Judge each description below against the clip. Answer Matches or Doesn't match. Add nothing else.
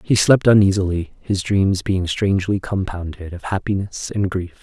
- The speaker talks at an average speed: Matches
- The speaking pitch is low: Matches